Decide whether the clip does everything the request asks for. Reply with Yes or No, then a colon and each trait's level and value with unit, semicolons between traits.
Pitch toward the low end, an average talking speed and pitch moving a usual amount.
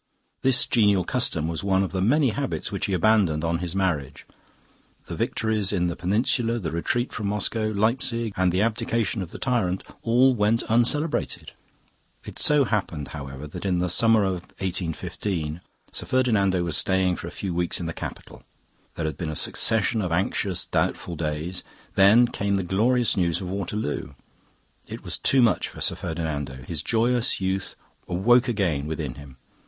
Yes: very low, 95 Hz; average, 170 wpm; average, 5.0 semitones